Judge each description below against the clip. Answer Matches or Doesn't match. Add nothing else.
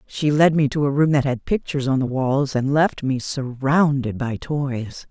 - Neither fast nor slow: Doesn't match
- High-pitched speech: Doesn't match